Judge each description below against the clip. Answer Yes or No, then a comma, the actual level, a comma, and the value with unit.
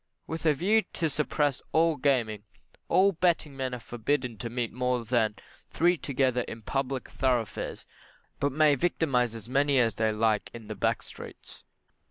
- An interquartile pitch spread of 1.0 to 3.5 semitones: No, average, 4.3 semitones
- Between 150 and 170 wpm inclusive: Yes, average, 165 wpm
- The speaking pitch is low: Yes, low, 130 Hz